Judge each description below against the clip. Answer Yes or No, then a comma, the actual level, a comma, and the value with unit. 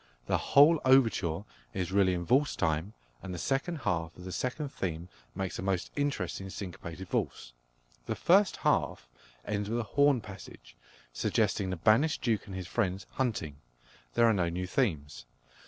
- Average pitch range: No, wide, 6.2 semitones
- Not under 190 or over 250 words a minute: No, average, 165 wpm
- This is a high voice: No, very low, 95 Hz